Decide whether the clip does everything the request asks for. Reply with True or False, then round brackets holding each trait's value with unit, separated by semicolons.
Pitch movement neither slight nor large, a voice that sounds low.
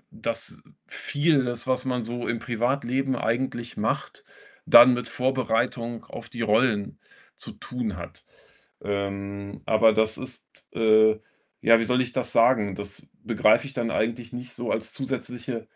False (2.3 semitones; 120 Hz)